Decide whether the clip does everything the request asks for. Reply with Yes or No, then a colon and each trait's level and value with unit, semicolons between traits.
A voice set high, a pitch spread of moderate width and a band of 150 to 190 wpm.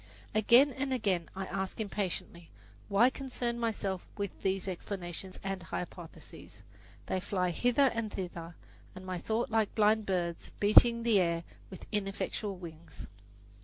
No: high, 195 Hz; average, 3.6 semitones; slow, 135 wpm